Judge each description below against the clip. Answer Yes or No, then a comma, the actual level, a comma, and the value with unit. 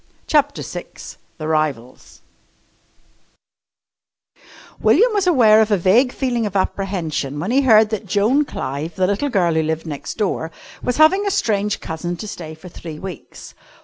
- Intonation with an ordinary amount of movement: No, wide, 7.2 semitones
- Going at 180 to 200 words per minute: No, average, 155 wpm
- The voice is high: Yes, high, 195 Hz